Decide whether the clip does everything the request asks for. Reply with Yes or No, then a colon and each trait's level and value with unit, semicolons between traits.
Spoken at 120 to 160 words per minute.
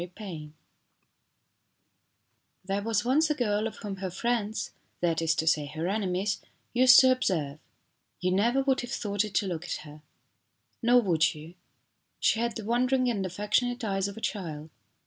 No: average, 175 wpm